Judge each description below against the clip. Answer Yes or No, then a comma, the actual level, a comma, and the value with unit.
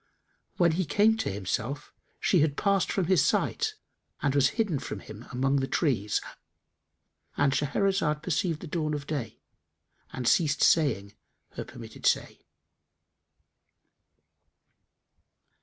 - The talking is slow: Yes, slow, 120 wpm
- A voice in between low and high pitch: Yes, medium, 150 Hz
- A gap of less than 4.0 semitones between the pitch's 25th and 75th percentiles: No, average, 4.8 semitones